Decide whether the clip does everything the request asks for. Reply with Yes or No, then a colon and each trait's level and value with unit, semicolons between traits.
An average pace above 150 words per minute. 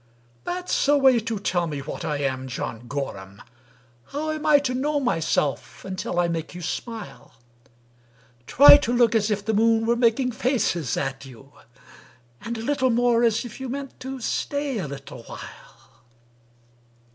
Yes: average, 170 wpm